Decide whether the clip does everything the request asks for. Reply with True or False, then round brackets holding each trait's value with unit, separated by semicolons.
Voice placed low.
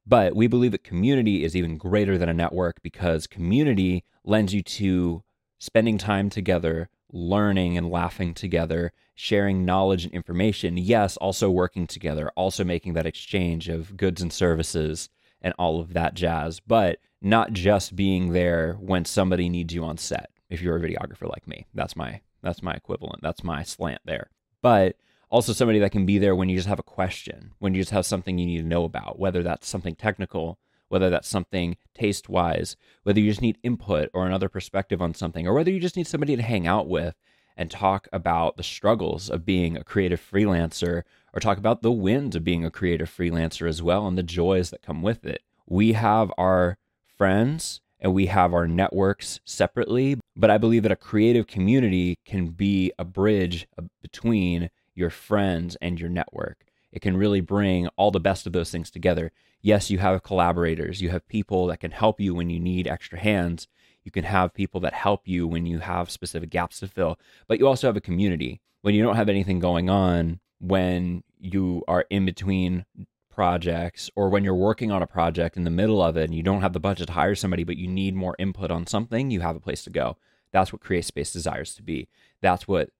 True (95 Hz)